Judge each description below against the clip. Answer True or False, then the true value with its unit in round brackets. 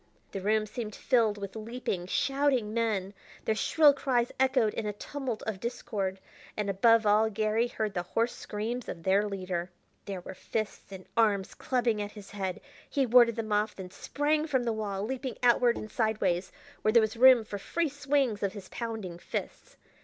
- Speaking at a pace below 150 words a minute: False (185 wpm)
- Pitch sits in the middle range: False (220 Hz)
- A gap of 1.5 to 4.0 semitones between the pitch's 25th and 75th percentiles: True (3.3 semitones)